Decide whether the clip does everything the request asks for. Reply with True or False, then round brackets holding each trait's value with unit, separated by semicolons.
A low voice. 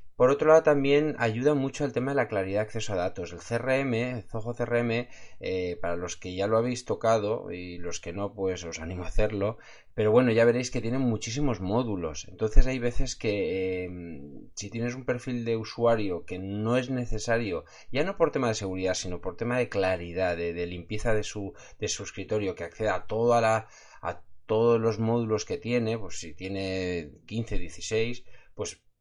True (110 Hz)